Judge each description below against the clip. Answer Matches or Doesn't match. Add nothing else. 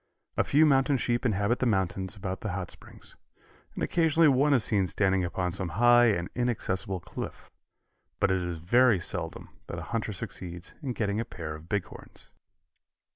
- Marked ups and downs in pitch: Doesn't match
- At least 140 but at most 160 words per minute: Doesn't match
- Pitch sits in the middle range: Doesn't match